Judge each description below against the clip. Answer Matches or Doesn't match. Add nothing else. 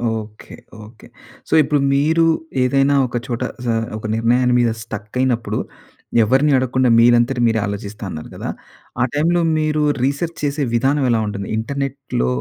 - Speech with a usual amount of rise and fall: Matches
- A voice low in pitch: Matches